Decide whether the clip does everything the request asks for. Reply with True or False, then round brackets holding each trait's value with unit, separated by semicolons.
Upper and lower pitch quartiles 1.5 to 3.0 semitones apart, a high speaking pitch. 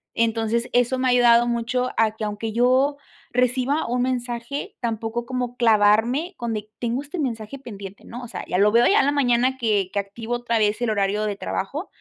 True (2.5 semitones; 235 Hz)